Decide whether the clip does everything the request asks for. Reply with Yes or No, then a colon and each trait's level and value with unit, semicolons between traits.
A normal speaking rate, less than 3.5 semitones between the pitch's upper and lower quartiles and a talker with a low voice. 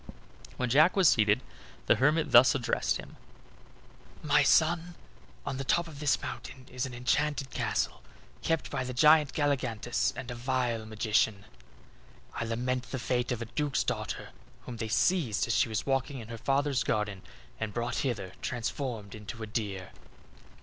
No: average, 165 wpm; average, 3.9 semitones; low, 125 Hz